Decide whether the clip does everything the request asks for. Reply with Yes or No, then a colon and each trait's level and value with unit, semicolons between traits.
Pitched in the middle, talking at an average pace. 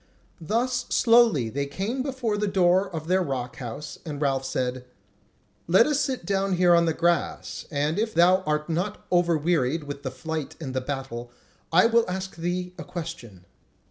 Yes: medium, 170 Hz; average, 175 wpm